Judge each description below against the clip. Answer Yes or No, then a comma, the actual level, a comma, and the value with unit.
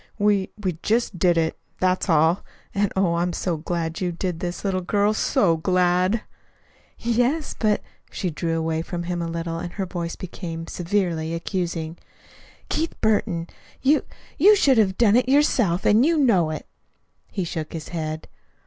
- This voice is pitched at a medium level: Yes, medium, 180 Hz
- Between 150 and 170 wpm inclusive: Yes, average, 165 wpm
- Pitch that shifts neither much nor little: Yes, average, 3.9 semitones